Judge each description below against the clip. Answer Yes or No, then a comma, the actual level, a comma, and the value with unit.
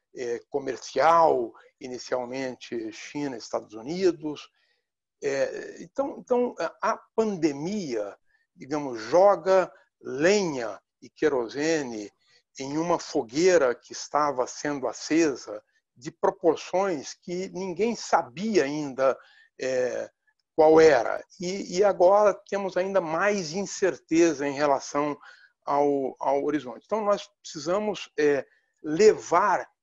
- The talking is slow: Yes, slow, 100 wpm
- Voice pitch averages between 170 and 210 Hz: Yes, medium, 185 Hz